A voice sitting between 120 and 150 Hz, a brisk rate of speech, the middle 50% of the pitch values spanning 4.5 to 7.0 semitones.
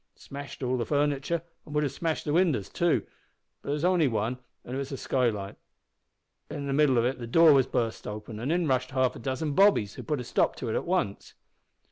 No: low, 135 Hz; fast, 230 wpm; average, 3.8 semitones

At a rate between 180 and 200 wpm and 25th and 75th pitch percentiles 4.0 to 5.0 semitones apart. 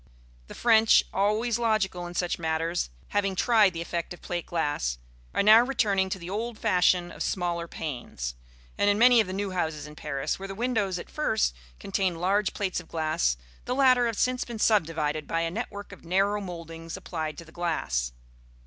Yes: average, 190 wpm; average, 4.3 semitones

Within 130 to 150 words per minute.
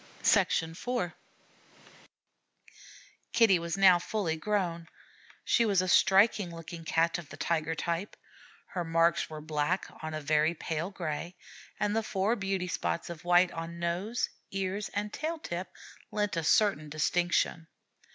Yes: average, 140 wpm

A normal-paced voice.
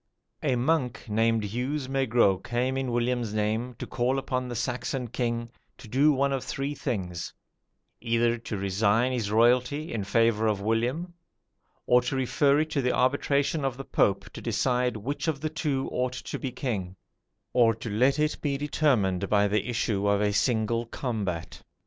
Yes: average, 175 wpm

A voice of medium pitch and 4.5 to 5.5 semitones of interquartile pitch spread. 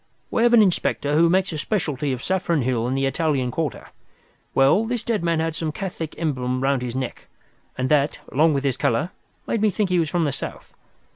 Yes: medium, 155 Hz; average, 5.0 semitones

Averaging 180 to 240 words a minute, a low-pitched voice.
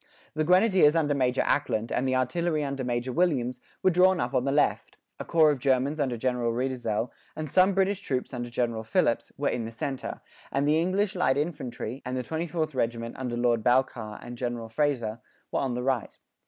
Yes: average, 195 wpm; low, 130 Hz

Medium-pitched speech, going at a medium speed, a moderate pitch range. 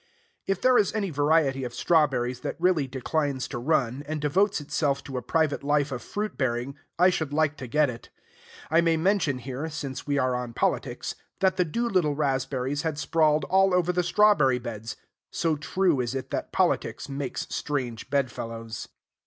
Yes: medium, 145 Hz; average, 180 wpm; average, 4.2 semitones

